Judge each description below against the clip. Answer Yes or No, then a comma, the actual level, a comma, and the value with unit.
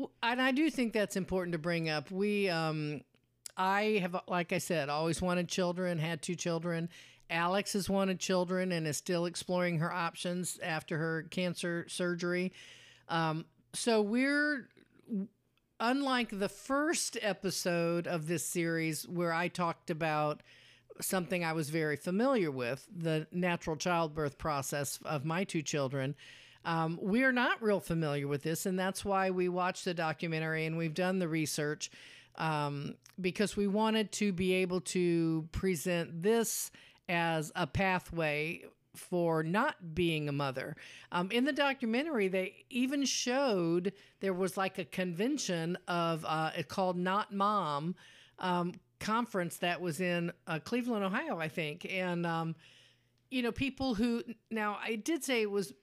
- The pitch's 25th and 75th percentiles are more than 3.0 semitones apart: Yes, average, 3.6 semitones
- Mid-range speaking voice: Yes, medium, 180 Hz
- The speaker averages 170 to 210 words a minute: No, average, 150 wpm